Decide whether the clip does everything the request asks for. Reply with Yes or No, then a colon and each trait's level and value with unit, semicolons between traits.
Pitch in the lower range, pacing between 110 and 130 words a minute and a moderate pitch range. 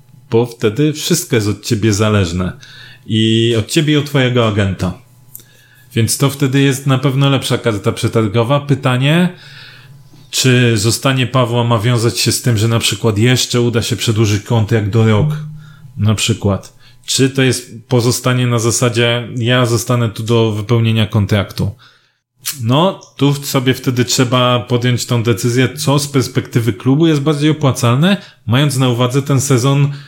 No: low, 125 Hz; average, 155 wpm; average, 3.0 semitones